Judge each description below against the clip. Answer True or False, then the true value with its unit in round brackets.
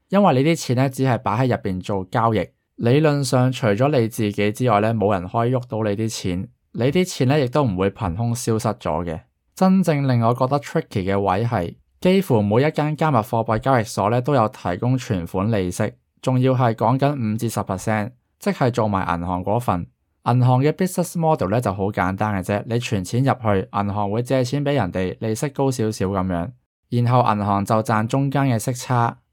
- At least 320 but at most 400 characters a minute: True (330 characters per minute)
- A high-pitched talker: False (115 Hz)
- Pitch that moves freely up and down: False (4.4 semitones)